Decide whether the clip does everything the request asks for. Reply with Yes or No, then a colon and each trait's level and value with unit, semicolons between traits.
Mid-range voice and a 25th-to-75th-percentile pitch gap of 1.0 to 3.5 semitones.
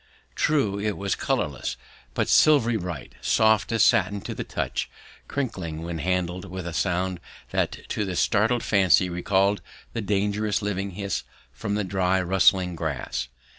No: very low, 95 Hz; narrow, 2.6 semitones